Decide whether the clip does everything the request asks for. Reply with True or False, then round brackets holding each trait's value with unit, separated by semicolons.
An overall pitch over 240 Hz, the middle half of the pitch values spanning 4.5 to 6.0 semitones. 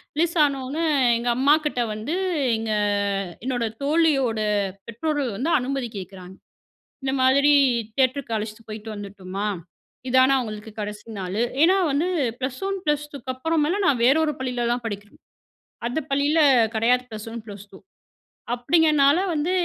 True (255 Hz; 5.1 semitones)